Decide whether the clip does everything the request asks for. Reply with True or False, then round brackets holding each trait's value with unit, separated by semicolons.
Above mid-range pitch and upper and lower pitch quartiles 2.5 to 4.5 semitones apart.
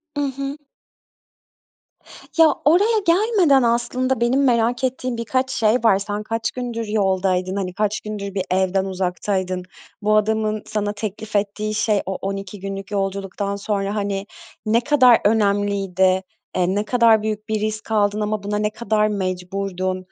True (210 Hz; 2.8 semitones)